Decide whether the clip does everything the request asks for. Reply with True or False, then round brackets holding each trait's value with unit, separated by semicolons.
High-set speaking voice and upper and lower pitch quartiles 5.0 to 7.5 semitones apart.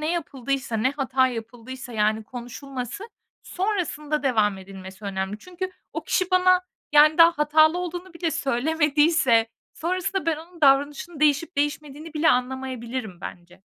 True (285 Hz; 5.5 semitones)